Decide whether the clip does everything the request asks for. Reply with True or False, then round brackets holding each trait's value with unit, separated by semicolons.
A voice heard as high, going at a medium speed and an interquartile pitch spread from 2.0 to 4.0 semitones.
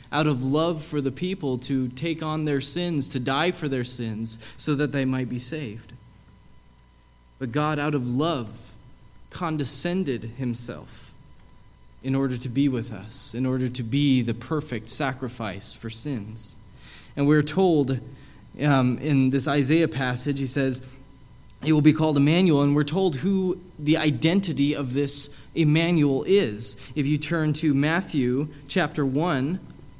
False (140 Hz; 150 wpm; 3.5 semitones)